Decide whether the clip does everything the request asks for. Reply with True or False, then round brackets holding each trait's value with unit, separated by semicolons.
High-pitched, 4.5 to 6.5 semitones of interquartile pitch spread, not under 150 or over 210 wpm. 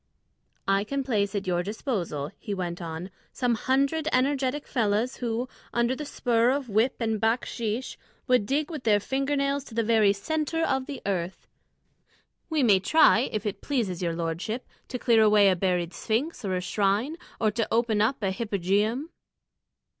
True (225 Hz; 4.9 semitones; 170 wpm)